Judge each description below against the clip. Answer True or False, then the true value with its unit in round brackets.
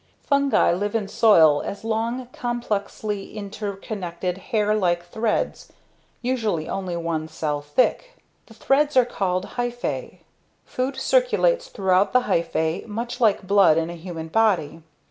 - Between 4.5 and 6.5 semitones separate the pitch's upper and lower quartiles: True (5.6 semitones)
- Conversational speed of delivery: False (130 wpm)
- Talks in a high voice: True (205 Hz)